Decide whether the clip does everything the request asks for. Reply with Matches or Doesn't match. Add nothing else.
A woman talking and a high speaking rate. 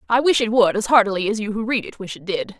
Matches